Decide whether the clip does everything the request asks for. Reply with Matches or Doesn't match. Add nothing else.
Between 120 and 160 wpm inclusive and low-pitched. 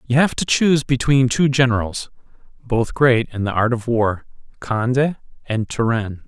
Matches